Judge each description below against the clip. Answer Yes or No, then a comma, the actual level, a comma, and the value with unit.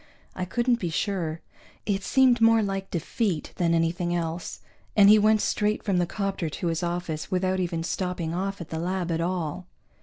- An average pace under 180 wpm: No, average, 185 wpm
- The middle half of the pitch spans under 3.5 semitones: Yes, average, 3.0 semitones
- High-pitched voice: No, medium, 180 Hz